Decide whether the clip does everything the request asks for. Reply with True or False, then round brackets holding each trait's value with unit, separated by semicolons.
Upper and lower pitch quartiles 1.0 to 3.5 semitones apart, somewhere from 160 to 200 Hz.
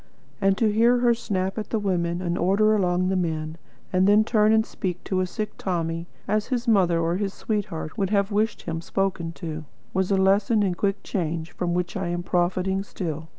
True (3.2 semitones; 190 Hz)